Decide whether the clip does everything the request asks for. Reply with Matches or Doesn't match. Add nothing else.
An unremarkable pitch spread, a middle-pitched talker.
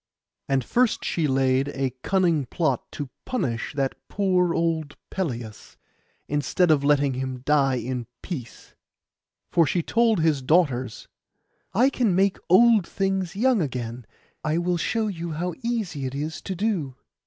Doesn't match